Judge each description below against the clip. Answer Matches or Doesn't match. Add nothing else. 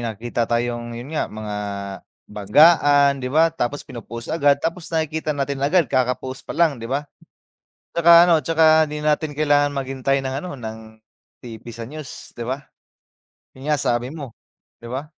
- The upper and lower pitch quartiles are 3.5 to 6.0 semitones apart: Matches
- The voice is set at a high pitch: Doesn't match